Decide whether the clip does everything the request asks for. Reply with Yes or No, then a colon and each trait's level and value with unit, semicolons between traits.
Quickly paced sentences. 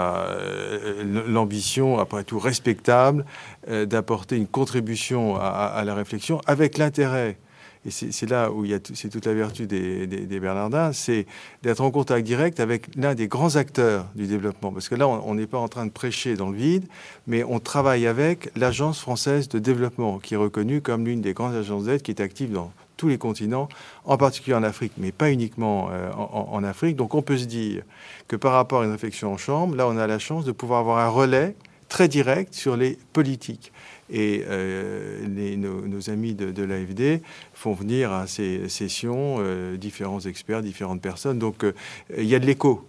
No: average, 205 wpm